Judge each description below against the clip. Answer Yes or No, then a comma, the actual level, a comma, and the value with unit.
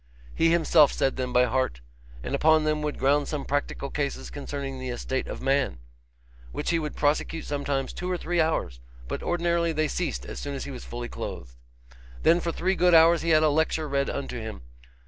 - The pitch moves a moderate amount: Yes, average, 3.5 semitones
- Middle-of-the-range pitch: Yes, medium, 145 Hz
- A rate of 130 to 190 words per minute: No, fast, 205 wpm